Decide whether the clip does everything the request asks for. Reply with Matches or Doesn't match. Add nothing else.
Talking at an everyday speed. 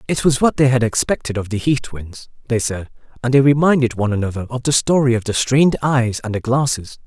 Doesn't match